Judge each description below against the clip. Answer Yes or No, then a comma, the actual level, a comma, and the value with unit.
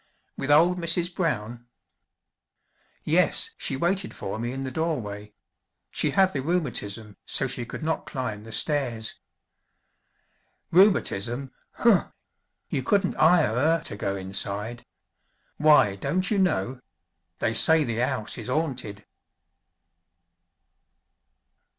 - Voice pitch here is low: Yes, low, 130 Hz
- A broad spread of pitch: Yes, wide, 6.7 semitones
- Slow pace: Yes, slow, 115 wpm